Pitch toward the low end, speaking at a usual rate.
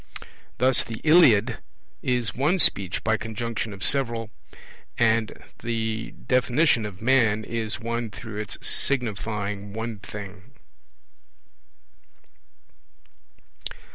No: low, 115 Hz; slow, 95 wpm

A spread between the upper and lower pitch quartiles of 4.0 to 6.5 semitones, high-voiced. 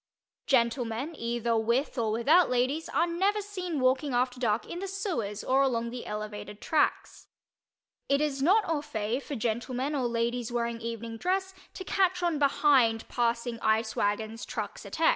Yes: average, 4.8 semitones; very high, 250 Hz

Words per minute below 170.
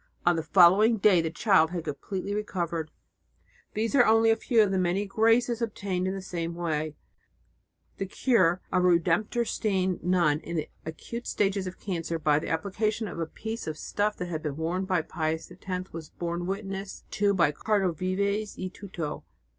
No: average, 180 wpm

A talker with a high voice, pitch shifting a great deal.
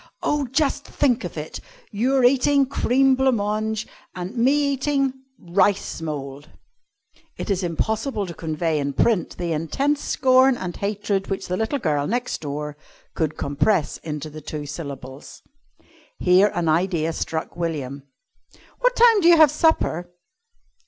Yes: high, 200 Hz; wide, 8.9 semitones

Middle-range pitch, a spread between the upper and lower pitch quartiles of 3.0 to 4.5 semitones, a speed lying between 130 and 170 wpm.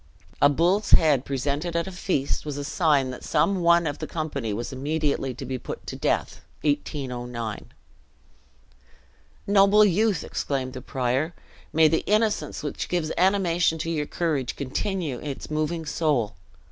Yes: medium, 150 Hz; average, 4.2 semitones; average, 150 wpm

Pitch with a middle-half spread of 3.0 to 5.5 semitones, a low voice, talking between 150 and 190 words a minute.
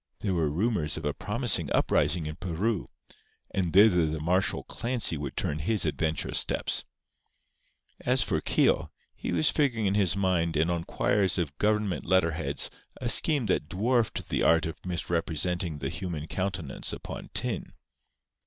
Yes: average, 4.0 semitones; very low, 90 Hz; average, 155 wpm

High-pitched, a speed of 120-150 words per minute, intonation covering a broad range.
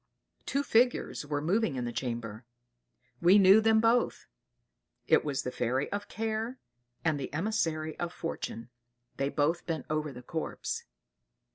No: medium, 160 Hz; average, 145 wpm; wide, 7.9 semitones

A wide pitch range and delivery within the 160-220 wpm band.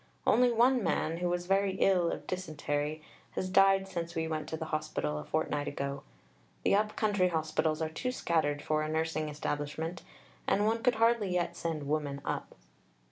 No: average, 4.0 semitones; average, 180 wpm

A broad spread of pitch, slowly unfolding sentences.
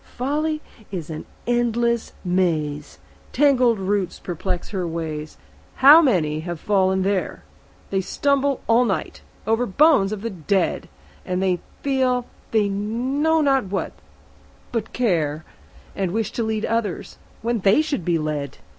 Yes: wide, 5.7 semitones; slow, 130 wpm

